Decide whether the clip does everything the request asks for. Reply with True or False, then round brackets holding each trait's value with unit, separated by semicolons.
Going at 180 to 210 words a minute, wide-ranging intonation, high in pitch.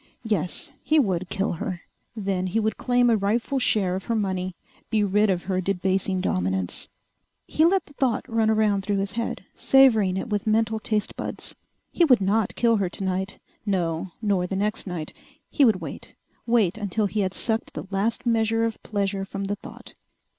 False (185 wpm; 3.1 semitones; 205 Hz)